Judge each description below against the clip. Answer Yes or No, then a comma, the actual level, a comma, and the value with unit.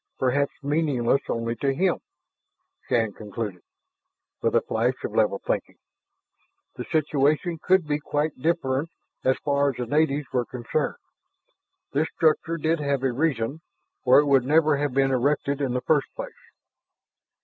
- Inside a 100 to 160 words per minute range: Yes, average, 150 wpm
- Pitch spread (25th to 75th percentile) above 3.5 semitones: No, average, 3.2 semitones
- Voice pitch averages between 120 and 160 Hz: Yes, medium, 140 Hz